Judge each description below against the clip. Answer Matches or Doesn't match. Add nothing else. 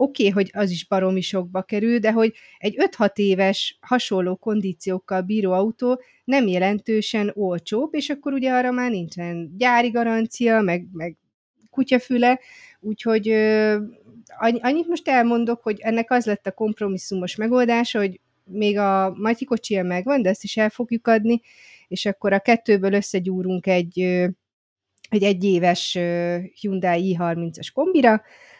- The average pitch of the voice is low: Doesn't match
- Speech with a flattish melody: Doesn't match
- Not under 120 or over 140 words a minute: Matches